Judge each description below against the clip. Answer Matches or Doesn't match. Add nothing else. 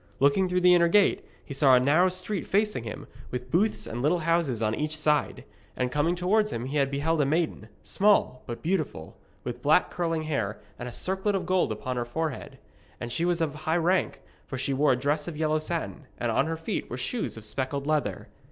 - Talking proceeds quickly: Matches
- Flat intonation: Doesn't match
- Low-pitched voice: Doesn't match